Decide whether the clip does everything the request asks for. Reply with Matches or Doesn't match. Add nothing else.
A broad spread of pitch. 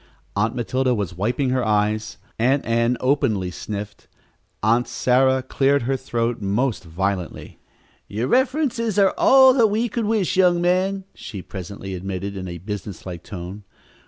Matches